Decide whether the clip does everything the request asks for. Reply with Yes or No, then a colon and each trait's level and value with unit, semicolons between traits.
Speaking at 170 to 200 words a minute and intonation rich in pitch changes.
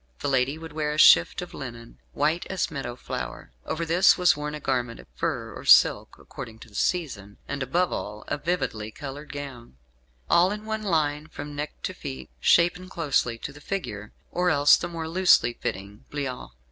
Yes: average, 190 wpm; wide, 6.0 semitones